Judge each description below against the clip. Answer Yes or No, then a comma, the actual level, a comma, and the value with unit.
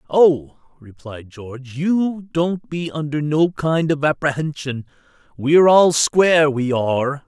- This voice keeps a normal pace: No, slow, 130 wpm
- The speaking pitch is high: No, medium, 150 Hz